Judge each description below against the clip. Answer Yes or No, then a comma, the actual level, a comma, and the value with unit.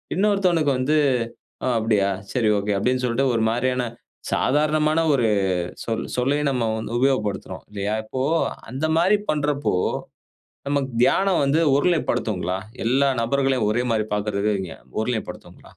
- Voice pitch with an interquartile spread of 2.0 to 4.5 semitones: No, average, 5.0 semitones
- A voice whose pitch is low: Yes, low, 130 Hz